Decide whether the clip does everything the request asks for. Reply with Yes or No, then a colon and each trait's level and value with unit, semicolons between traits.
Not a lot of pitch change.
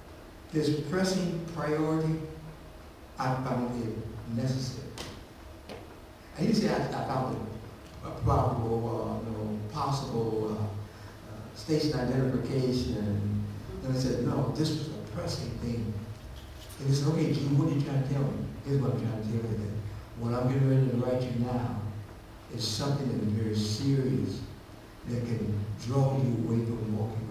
No: average, 4.1 semitones